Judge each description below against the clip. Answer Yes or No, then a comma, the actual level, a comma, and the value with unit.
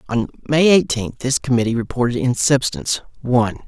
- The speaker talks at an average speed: Yes, average, 145 wpm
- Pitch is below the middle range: Yes, low, 130 Hz